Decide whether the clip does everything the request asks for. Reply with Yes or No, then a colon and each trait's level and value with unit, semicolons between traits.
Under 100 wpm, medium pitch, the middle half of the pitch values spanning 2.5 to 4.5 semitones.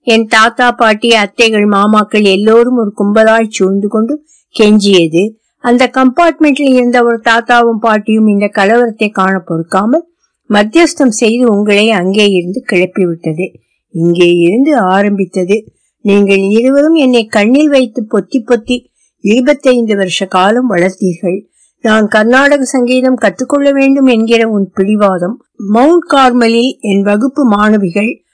No: average, 80 wpm; high, 225 Hz; average, 3.9 semitones